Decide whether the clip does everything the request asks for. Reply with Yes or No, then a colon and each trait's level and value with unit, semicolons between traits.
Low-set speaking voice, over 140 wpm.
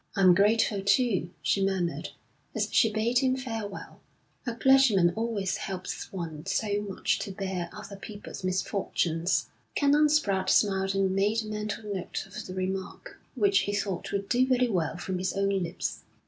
No: high, 200 Hz; average, 160 wpm